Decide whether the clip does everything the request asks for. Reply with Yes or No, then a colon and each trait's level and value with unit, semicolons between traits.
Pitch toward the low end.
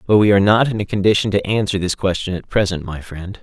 Yes: low, 100 Hz